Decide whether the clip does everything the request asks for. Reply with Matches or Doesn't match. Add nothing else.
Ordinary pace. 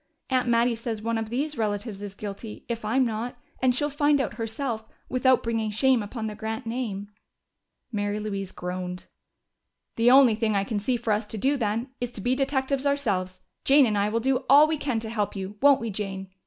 Doesn't match